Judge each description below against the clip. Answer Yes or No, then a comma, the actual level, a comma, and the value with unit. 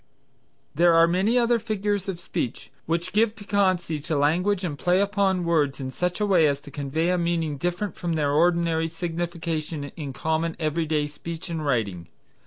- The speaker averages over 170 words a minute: Yes, average, 180 wpm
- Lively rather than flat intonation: No, average, 2.9 semitones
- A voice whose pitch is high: No, medium, 170 Hz